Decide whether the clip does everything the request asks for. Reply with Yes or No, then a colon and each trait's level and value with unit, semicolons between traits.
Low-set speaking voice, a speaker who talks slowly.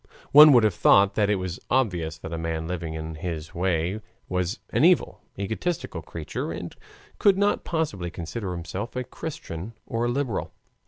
No: very low, 95 Hz; average, 170 wpm